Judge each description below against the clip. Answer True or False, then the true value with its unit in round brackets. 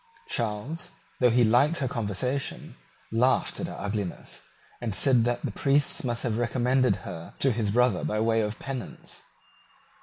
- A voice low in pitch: True (120 Hz)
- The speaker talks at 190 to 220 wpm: False (155 wpm)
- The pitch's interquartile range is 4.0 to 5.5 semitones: False (3.2 semitones)